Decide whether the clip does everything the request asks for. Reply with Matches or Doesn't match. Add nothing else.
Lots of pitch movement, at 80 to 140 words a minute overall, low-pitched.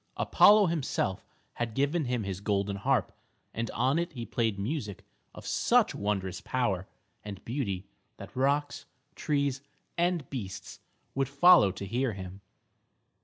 Matches